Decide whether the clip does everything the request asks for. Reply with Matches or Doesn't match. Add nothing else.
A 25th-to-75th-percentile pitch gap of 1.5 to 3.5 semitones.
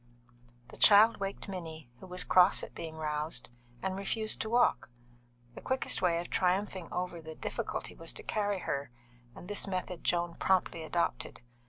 Matches